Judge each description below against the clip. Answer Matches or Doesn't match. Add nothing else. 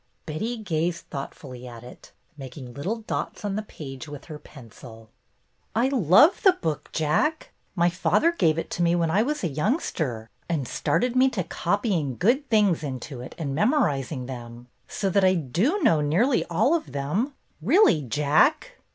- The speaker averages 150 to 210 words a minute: Matches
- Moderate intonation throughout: Doesn't match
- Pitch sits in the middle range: Matches